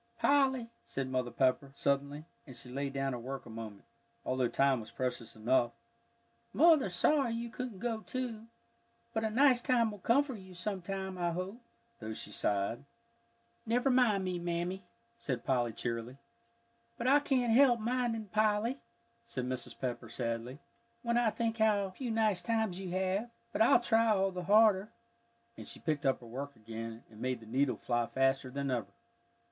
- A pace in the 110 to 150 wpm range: No, average, 175 wpm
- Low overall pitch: No, medium, 185 Hz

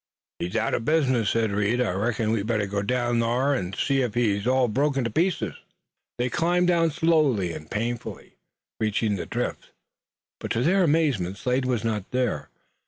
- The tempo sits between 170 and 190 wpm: Yes, average, 175 wpm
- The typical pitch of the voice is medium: No, low, 120 Hz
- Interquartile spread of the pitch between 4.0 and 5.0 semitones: Yes, average, 4.6 semitones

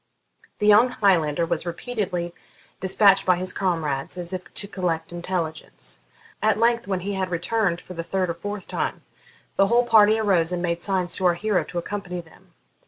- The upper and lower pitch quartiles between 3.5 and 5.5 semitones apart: No, average, 3.0 semitones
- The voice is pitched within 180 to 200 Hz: Yes, medium, 185 Hz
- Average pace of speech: Yes, average, 180 wpm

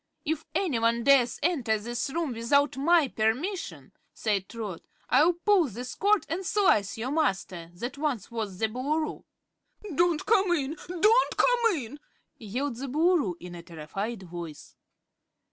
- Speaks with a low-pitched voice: No, very high, 265 Hz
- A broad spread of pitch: Yes, wide, 7.2 semitones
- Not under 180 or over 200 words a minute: No, average, 145 wpm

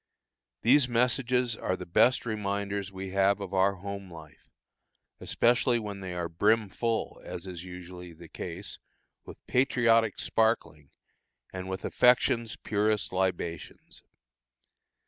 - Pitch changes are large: No, average, 3.9 semitones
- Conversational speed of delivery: No, slow, 125 wpm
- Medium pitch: No, low, 100 Hz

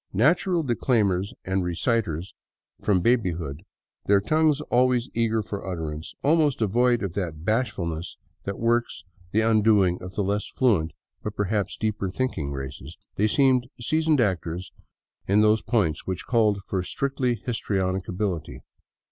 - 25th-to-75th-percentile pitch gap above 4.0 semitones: Yes, average, 4.8 semitones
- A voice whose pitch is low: Yes, low, 105 Hz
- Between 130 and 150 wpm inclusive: Yes, average, 140 wpm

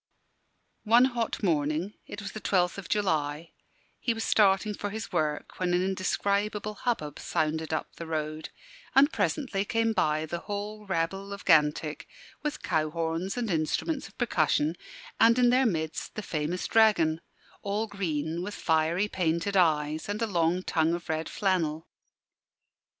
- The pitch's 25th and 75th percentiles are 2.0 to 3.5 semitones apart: No, average, 4.8 semitones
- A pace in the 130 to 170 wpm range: Yes, average, 155 wpm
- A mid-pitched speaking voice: Yes, medium, 180 Hz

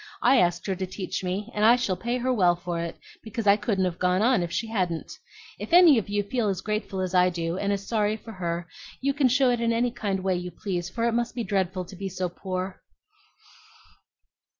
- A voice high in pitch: Yes, high, 195 Hz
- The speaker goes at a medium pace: No, fast, 235 wpm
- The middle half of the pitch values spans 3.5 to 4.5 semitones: Yes, average, 4.0 semitones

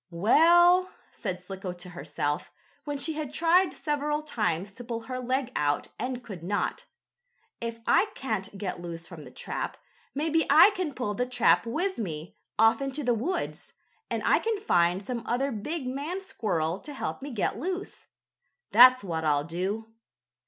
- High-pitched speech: Yes, high, 245 Hz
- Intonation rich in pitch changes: Yes, wide, 8.0 semitones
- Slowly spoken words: No, average, 165 wpm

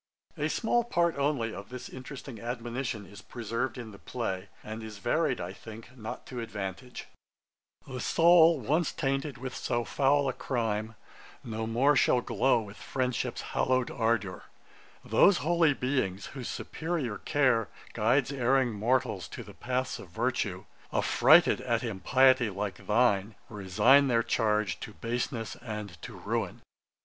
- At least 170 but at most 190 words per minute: No, average, 145 wpm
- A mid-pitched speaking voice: No, low, 120 Hz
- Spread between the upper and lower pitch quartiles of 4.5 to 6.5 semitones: No, average, 3.8 semitones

